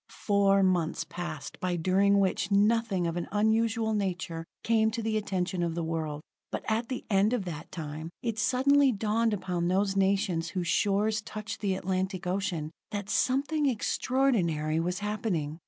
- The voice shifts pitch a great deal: No, average, 4.0 semitones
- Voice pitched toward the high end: Yes, high, 195 Hz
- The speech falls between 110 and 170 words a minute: Yes, average, 160 wpm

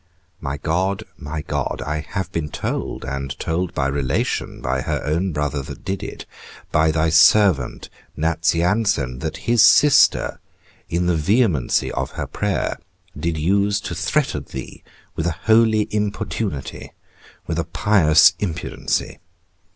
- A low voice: Yes, very low, 80 Hz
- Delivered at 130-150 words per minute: Yes, slow, 135 wpm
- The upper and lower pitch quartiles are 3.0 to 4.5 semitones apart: No, average, 4.9 semitones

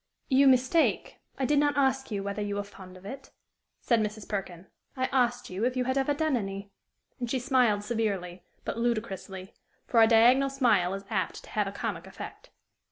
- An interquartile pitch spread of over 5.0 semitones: No, average, 4.7 semitones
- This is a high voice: Yes, high, 230 Hz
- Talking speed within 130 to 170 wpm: No, average, 195 wpm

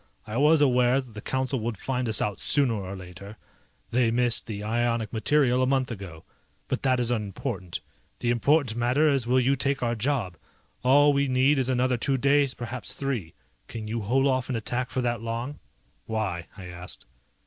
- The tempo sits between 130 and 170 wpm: No, average, 190 wpm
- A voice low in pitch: Yes, low, 120 Hz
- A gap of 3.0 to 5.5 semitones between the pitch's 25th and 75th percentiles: Yes, average, 3.4 semitones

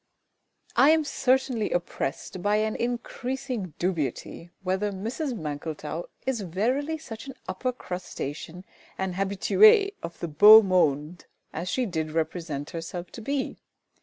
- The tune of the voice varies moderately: No, wide, 6.9 semitones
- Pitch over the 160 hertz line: Yes, high, 190 Hz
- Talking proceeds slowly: Yes, slow, 130 wpm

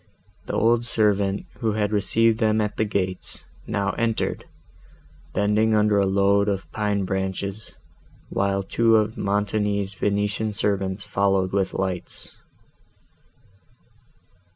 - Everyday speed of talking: No, slow, 115 wpm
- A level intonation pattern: Yes, narrow, 1.7 semitones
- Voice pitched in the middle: No, low, 100 Hz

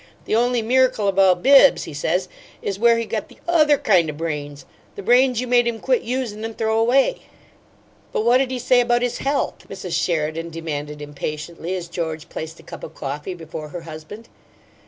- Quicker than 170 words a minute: Yes, average, 190 wpm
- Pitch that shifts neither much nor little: No, wide, 7.2 semitones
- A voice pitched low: No, high, 200 Hz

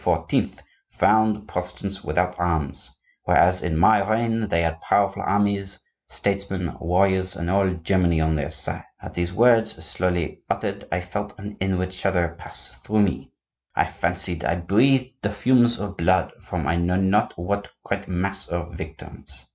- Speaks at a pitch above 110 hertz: No, very low, 95 Hz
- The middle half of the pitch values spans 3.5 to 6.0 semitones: No, average, 2.7 semitones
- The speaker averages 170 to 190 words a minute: No, average, 155 wpm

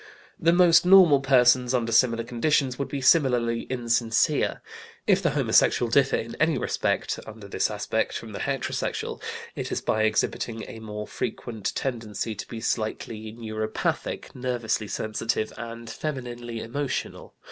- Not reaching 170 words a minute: Yes, average, 140 wpm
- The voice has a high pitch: No, low, 120 Hz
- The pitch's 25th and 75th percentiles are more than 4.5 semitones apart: No, average, 3.0 semitones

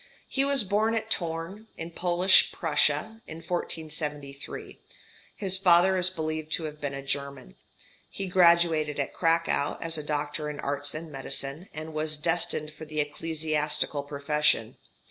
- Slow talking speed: No, average, 145 wpm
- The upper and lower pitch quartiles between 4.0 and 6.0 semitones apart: No, average, 2.8 semitones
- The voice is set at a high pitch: No, medium, 155 Hz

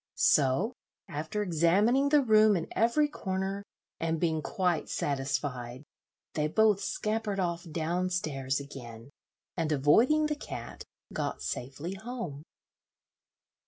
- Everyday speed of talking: No, slow, 115 wpm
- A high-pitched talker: No, medium, 175 Hz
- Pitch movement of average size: No, wide, 6.7 semitones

